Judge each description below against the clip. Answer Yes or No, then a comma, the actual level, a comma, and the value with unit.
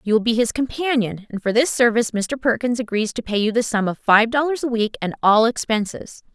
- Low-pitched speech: No, high, 230 Hz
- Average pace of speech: No, fast, 235 wpm